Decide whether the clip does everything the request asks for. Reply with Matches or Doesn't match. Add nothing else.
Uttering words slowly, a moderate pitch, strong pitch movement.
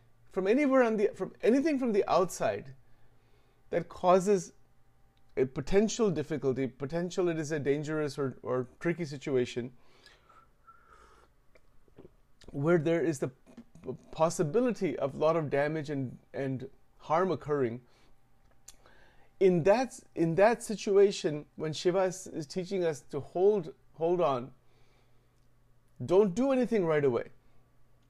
Matches